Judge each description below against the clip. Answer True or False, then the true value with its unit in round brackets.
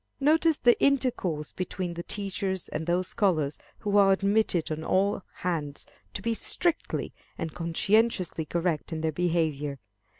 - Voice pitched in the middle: True (180 Hz)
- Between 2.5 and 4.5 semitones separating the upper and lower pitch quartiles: True (4.2 semitones)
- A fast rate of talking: False (140 wpm)